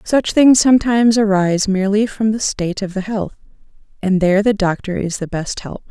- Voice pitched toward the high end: Yes, high, 205 Hz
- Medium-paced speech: Yes, average, 195 wpm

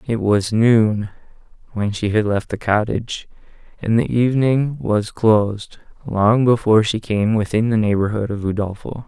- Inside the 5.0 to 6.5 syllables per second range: No, 4.6 syllables/s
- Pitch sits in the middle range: No, low, 110 Hz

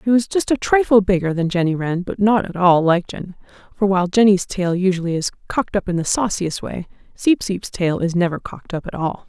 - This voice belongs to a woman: Yes, female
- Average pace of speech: No, fast, 235 wpm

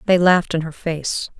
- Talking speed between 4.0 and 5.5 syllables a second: Yes, 5.1 syllables/s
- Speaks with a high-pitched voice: No, medium, 170 Hz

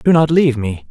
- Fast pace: Yes, fast, 265 wpm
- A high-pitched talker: No, medium, 140 Hz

